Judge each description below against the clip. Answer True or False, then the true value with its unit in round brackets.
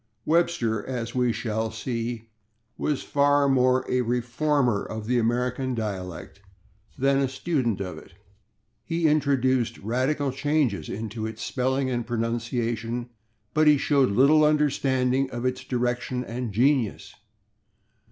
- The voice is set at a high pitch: False (125 Hz)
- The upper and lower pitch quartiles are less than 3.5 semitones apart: True (3.0 semitones)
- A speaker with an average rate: False (125 wpm)